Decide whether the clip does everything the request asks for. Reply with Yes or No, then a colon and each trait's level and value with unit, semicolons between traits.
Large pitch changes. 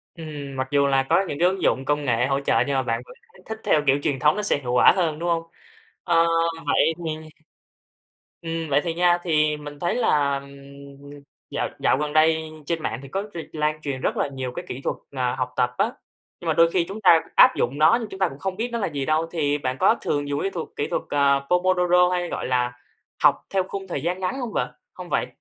No: average, 4.0 semitones